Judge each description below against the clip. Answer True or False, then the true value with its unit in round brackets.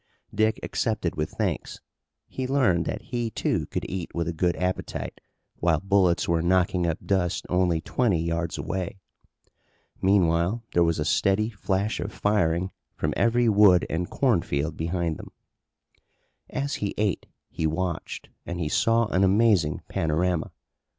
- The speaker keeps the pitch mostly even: False (3.9 semitones)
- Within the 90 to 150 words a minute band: True (145 wpm)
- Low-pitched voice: True (90 Hz)